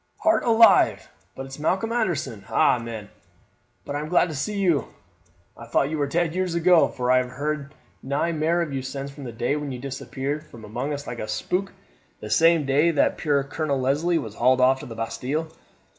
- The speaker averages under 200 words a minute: No, fast, 205 wpm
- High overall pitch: No, medium, 140 Hz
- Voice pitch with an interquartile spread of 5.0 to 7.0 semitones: No, average, 4.3 semitones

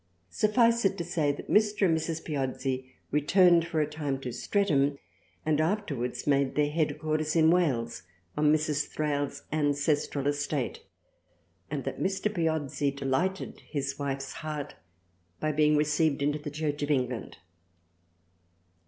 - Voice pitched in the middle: Yes, medium, 150 Hz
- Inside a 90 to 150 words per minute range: Yes, slow, 135 wpm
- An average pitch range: No, narrow, 2.3 semitones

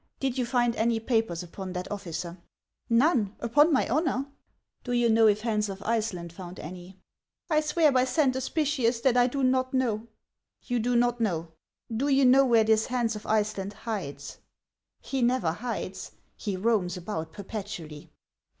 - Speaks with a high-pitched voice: Yes, high, 225 Hz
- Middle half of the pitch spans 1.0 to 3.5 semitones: No, average, 4.7 semitones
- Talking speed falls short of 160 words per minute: No, average, 190 wpm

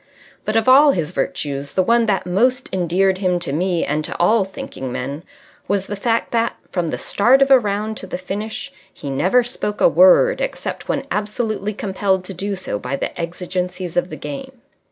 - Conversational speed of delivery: Yes, average, 195 wpm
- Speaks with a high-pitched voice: Yes, high, 195 Hz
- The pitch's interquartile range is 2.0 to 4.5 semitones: Yes, average, 4.2 semitones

